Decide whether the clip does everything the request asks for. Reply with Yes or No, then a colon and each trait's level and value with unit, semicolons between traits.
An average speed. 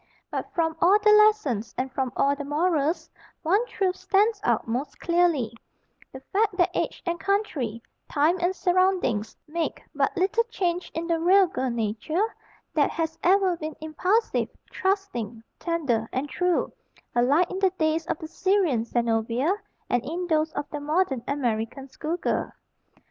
Yes: average, 155 wpm